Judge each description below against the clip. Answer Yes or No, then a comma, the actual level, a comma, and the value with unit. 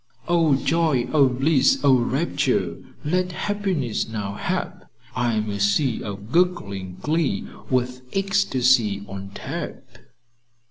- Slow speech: Yes, slow, 120 wpm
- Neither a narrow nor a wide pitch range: No, wide, 7.4 semitones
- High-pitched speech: No, low, 130 Hz